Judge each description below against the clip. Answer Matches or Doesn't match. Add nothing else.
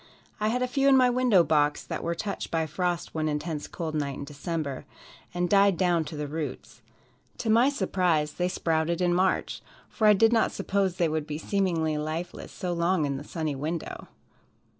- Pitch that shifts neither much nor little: Matches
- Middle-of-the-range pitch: Matches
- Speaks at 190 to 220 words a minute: Matches